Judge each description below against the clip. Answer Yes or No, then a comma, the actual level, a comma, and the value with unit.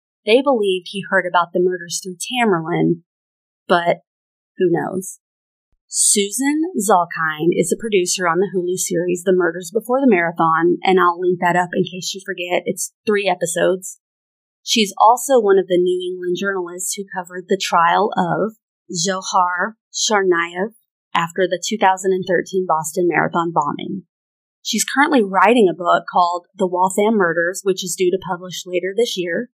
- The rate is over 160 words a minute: No, average, 155 wpm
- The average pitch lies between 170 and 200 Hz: Yes, medium, 185 Hz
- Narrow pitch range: Yes, narrow, 2.1 semitones